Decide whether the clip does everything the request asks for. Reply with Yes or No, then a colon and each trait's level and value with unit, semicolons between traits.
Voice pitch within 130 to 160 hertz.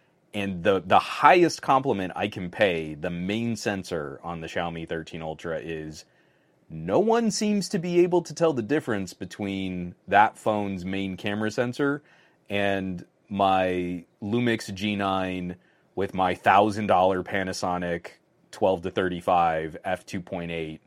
No: very low, 95 Hz